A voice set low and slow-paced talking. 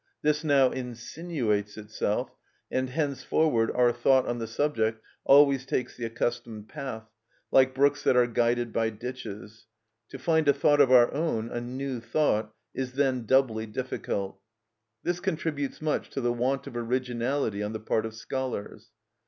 No: low, 125 Hz; average, 155 wpm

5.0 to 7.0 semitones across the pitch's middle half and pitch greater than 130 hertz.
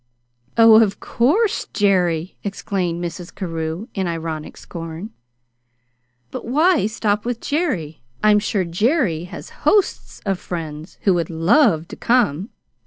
Yes: wide, 5.4 semitones; high, 190 Hz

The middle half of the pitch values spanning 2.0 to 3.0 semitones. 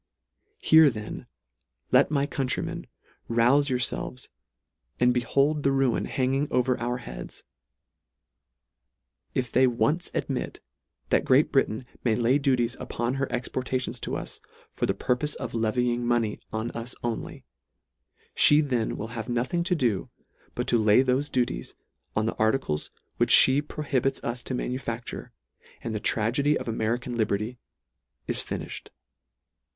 Yes: average, 2.7 semitones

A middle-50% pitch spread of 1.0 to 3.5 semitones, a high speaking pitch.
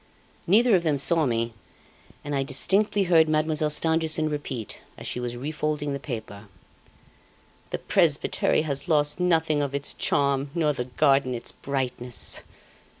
No: average, 3.2 semitones; medium, 145 Hz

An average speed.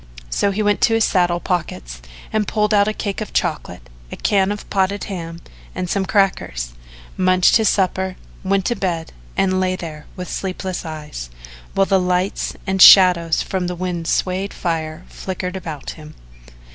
Yes: average, 170 wpm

